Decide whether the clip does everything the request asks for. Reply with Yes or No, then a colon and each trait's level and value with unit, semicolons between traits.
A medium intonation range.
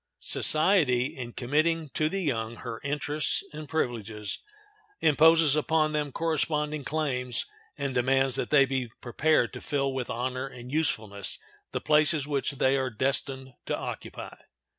Yes: average, 3.3 semitones